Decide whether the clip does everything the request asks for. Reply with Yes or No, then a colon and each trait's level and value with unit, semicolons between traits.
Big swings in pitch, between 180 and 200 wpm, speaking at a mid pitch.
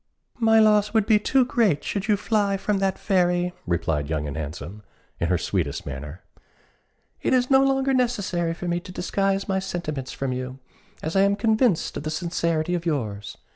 Yes: wide, 8.5 semitones; average, 185 wpm; medium, 180 Hz